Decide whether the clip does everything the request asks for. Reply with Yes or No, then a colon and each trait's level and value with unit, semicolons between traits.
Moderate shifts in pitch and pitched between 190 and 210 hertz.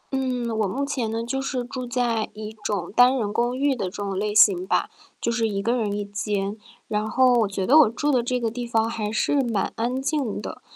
No: average, 3.2 semitones; high, 230 Hz